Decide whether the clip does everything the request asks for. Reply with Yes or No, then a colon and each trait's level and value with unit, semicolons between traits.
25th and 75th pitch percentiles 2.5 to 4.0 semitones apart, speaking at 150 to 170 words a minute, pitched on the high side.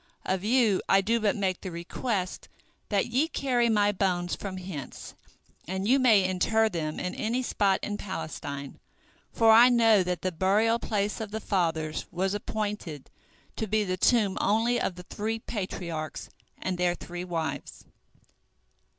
Yes: average, 3.6 semitones; average, 160 wpm; high, 195 Hz